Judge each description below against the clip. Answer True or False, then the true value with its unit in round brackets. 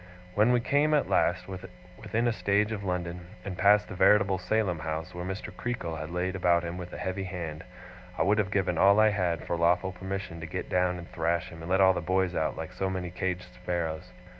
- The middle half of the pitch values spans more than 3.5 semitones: False (2.5 semitones)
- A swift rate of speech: True (225 wpm)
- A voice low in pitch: True (90 Hz)